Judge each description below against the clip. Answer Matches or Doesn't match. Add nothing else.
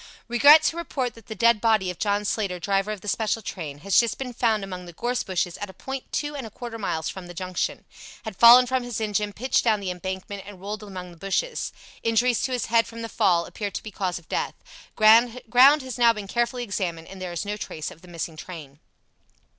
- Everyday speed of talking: Doesn't match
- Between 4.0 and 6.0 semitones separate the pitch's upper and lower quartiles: Matches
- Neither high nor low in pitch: Doesn't match